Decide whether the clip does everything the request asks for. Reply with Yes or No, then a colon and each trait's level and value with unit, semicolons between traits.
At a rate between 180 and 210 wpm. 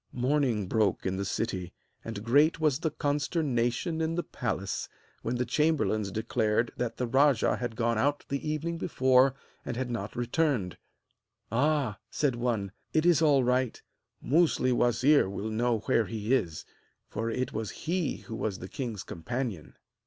No: average, 160 wpm